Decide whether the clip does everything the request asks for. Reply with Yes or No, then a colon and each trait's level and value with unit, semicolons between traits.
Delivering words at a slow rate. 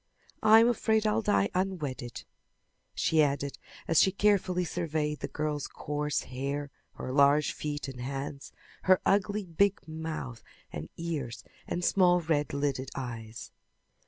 Yes: slow, 130 wpm